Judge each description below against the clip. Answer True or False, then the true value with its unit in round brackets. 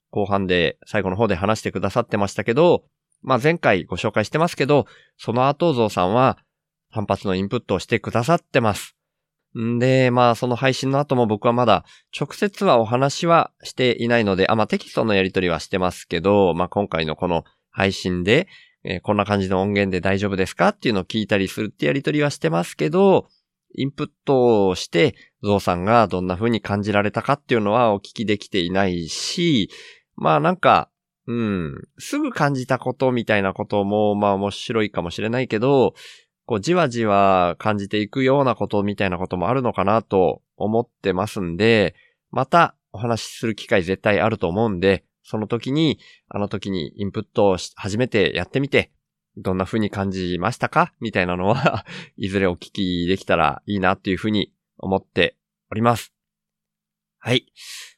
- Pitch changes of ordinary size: True (4.3 semitones)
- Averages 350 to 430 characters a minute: True (365 characters per minute)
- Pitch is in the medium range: False (105 Hz)